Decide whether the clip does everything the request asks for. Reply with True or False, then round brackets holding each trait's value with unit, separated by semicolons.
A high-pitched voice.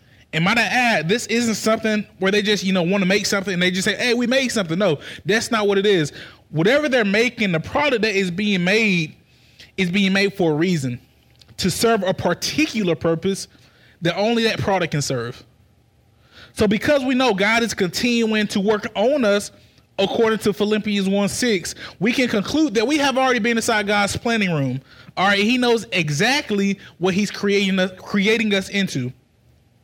True (200 Hz)